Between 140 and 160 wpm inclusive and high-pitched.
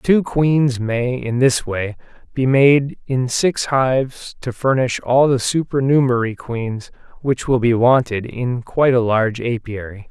No: average, 155 wpm; low, 125 Hz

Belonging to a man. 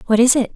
No: female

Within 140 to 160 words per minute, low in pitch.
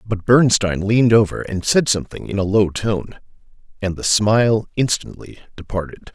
Yes: average, 155 wpm; low, 105 Hz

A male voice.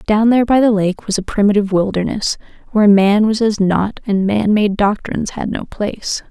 No: female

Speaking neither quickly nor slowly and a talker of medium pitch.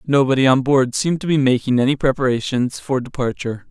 No: average, 180 wpm; low, 130 Hz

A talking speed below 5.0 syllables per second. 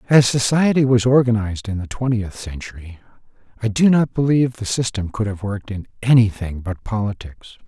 No: 5.6 syllables/s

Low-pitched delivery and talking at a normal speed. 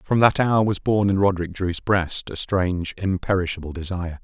Yes: very low, 95 Hz; average, 185 wpm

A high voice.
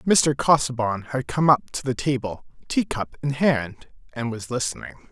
No: low, 135 Hz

